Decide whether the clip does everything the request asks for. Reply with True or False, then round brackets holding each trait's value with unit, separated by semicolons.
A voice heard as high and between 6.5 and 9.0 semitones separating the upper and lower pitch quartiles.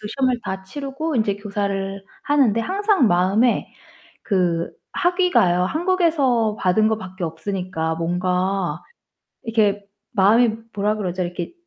False (205 Hz; 5.3 semitones)